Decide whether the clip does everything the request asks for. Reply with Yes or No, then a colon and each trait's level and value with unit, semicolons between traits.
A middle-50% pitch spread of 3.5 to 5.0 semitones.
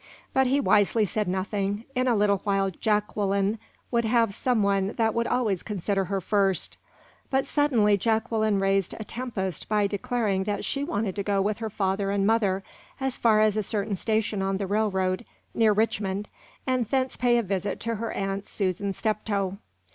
No: narrow, 2.4 semitones